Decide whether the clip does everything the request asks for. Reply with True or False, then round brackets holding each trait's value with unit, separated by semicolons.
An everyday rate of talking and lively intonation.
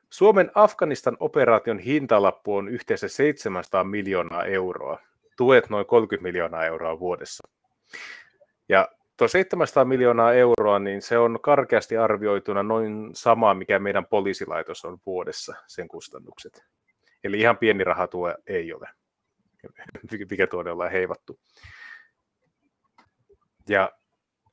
True (110 wpm; 6.1 semitones)